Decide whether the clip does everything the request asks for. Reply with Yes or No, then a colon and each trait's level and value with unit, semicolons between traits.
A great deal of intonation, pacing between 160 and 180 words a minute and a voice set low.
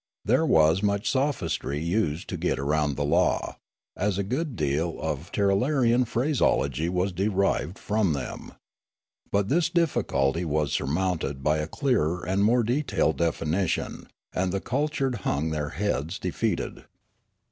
No: wide, 6.2 semitones; slow, 135 wpm; very low, 90 Hz